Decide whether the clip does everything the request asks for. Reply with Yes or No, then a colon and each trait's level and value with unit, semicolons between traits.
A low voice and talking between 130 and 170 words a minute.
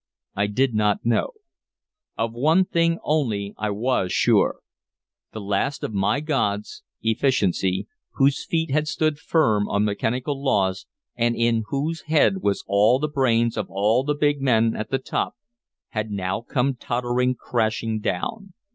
Yes: low, 120 Hz; average, 150 wpm